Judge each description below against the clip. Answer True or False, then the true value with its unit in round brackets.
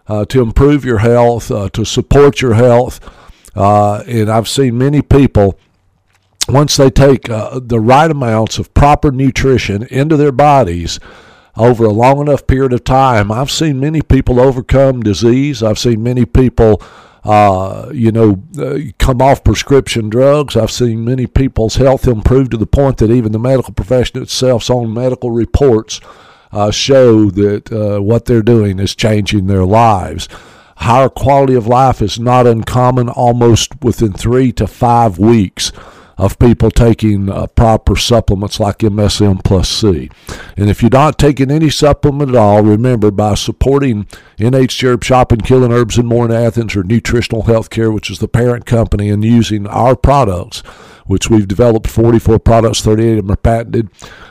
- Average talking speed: True (165 wpm)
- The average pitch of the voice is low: True (115 Hz)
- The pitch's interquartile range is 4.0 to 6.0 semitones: False (3.4 semitones)